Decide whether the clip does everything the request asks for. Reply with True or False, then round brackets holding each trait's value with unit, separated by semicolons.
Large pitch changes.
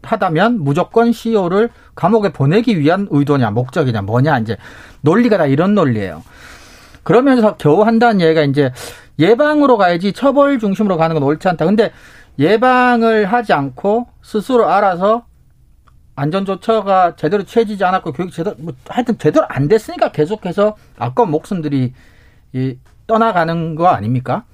True (7.6 semitones)